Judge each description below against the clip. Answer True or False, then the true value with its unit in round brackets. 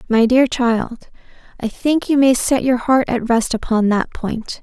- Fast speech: False (195 wpm)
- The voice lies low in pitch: False (240 Hz)